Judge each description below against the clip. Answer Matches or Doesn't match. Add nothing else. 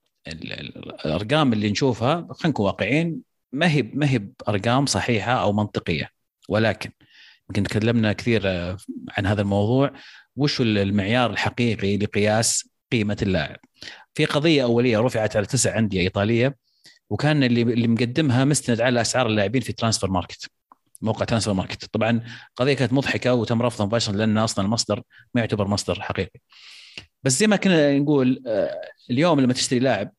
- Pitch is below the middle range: Matches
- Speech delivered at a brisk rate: Matches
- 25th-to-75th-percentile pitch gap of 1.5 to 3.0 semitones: Doesn't match